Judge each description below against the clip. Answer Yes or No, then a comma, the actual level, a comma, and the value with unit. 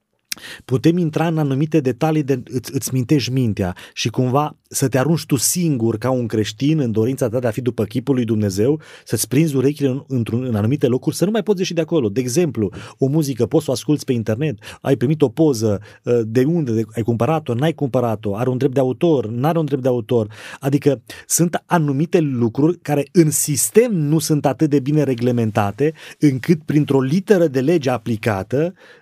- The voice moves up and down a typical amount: Yes, average, 4.6 semitones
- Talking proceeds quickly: Yes, fast, 195 wpm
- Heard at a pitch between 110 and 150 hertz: Yes, low, 135 Hz